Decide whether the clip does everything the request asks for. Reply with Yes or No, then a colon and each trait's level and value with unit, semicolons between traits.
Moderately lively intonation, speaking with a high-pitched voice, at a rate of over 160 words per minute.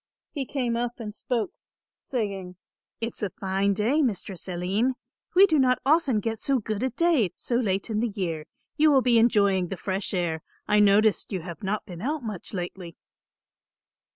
Yes: average, 4.7 semitones; high, 215 Hz; average, 180 wpm